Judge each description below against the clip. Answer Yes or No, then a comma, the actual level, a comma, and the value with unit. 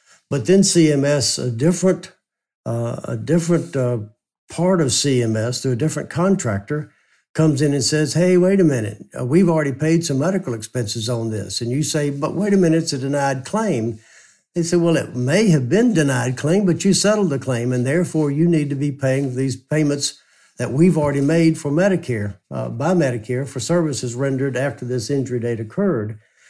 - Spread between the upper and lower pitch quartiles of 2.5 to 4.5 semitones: No, wide, 5.4 semitones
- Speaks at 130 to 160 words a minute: No, average, 190 wpm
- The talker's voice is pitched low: No, medium, 145 Hz